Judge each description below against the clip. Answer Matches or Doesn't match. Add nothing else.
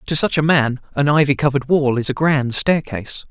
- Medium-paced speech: Doesn't match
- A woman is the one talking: Doesn't match